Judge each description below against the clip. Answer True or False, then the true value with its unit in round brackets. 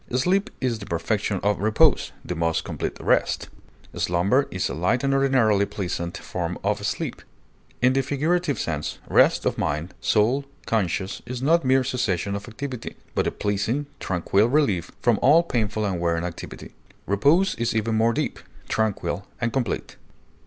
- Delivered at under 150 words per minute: False (160 wpm)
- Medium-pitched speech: False (110 Hz)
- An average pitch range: False (5.7 semitones)